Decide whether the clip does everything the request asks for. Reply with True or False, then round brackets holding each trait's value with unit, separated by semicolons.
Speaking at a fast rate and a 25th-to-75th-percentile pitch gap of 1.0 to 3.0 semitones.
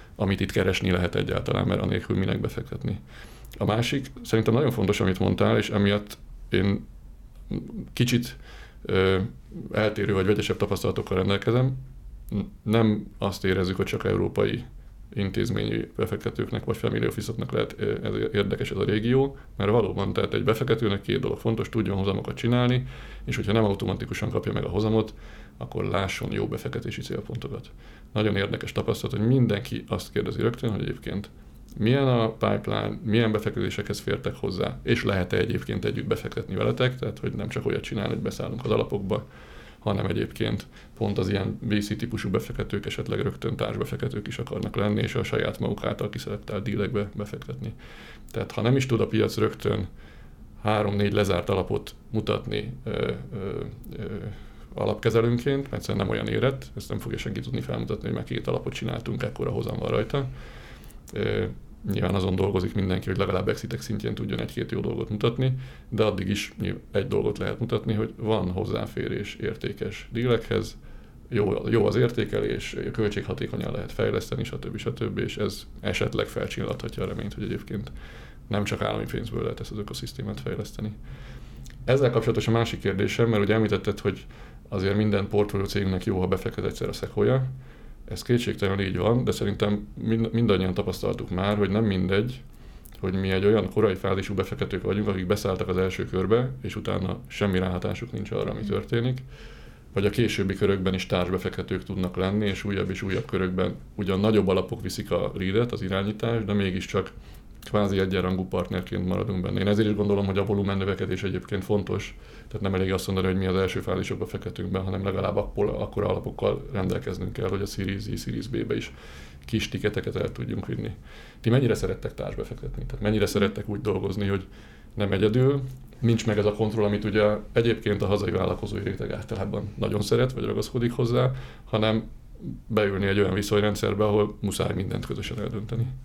True (165 wpm; 2.6 semitones)